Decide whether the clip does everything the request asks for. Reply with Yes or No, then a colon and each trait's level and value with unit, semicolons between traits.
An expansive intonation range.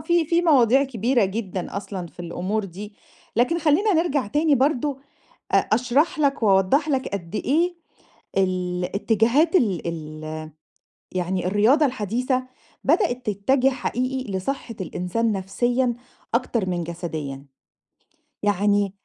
Yes: wide, 6.3 semitones